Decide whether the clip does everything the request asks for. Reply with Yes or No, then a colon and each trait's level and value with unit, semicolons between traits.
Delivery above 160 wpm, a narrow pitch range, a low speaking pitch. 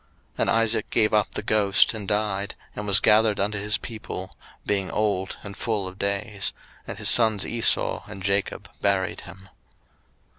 Yes: average, 170 wpm; narrow, 1.6 semitones; low, 105 Hz